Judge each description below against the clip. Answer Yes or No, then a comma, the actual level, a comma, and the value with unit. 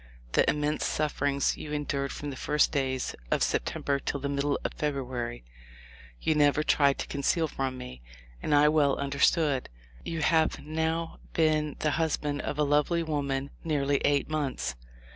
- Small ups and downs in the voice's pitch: Yes, narrow, 1.7 semitones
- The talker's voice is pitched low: No, medium, 145 Hz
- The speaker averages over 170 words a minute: No, average, 160 wpm